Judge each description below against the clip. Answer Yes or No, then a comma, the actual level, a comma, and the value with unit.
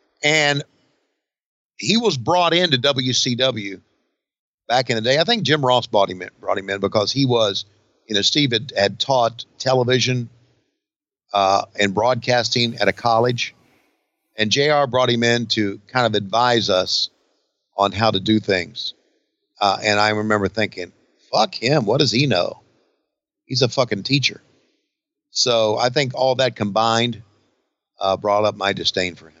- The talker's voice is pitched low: Yes, low, 120 Hz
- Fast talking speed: No, average, 160 wpm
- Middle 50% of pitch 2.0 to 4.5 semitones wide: Yes, average, 4.1 semitones